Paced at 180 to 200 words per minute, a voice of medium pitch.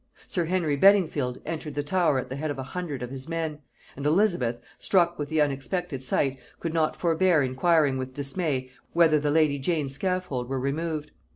Yes: average, 185 wpm; medium, 150 Hz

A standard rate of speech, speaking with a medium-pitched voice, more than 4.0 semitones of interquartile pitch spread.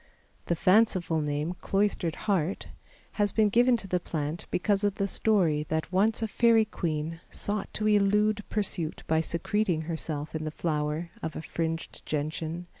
Yes: average, 160 wpm; medium, 175 Hz; average, 4.6 semitones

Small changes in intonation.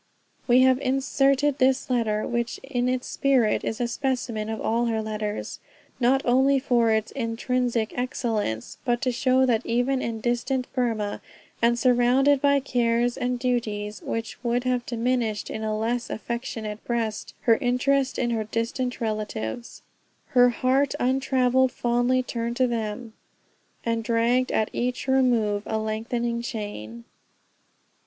Yes: narrow, 2.3 semitones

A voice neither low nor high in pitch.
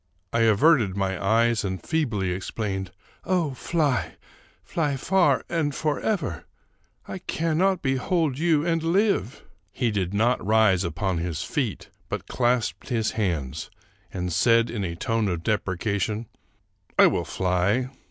No: low, 115 Hz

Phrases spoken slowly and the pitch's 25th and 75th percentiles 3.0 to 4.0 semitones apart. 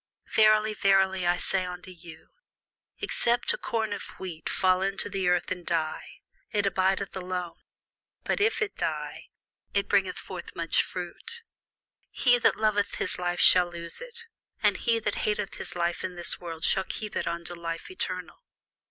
No: average, 165 wpm; average, 3.3 semitones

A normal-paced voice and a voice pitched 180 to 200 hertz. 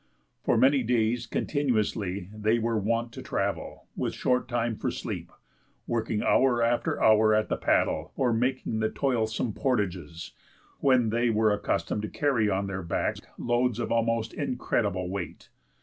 No: average, 150 wpm; low, 115 Hz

